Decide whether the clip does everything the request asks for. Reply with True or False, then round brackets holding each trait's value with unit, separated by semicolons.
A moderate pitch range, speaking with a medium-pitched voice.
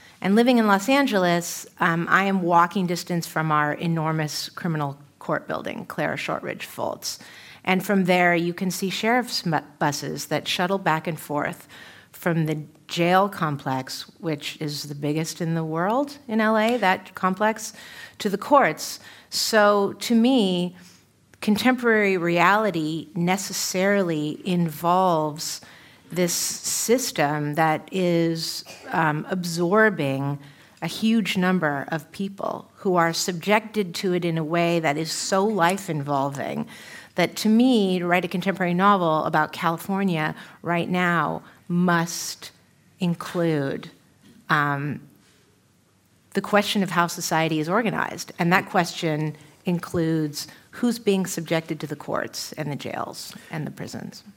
True (4.0 semitones; 175 Hz)